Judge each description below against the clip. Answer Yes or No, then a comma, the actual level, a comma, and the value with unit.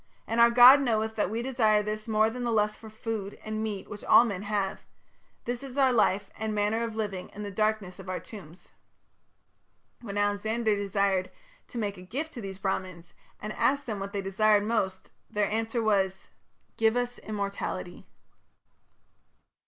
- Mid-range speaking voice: No, high, 215 Hz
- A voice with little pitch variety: Yes, narrow, 2.3 semitones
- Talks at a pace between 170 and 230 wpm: Yes, average, 175 wpm